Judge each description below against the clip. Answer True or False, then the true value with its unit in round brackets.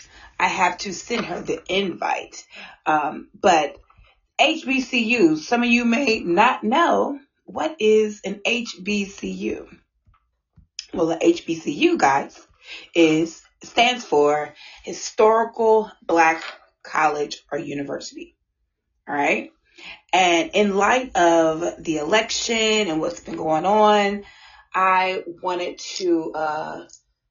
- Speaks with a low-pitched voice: False (210 Hz)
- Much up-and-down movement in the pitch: True (6.4 semitones)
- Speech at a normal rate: False (110 wpm)